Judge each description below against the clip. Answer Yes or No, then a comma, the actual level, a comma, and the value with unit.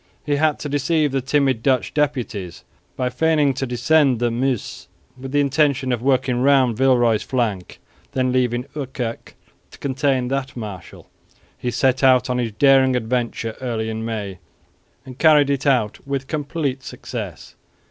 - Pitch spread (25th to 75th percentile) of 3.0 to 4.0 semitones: No, narrow, 2.6 semitones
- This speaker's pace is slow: No, average, 155 wpm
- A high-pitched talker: No, low, 130 Hz